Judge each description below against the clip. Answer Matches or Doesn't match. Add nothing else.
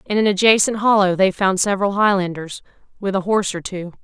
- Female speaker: Matches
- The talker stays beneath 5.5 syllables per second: Doesn't match